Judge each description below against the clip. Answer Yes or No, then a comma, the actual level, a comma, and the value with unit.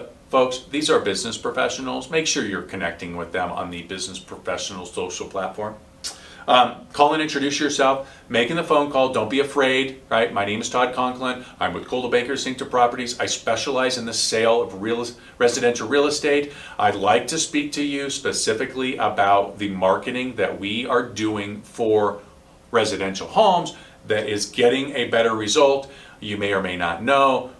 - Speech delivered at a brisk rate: No, average, 175 wpm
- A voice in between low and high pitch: No, low, 125 Hz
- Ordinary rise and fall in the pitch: Yes, average, 4.7 semitones